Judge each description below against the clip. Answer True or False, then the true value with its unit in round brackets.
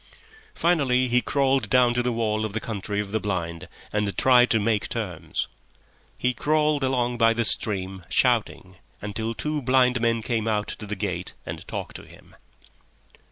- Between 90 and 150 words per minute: False (175 wpm)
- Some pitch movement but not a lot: True (3.2 semitones)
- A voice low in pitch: True (115 Hz)